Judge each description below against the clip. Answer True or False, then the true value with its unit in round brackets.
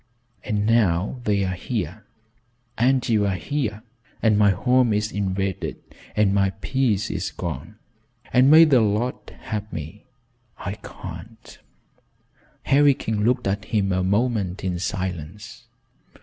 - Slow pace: True (125 wpm)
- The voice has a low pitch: True (105 Hz)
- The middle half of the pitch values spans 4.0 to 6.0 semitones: False (3.4 semitones)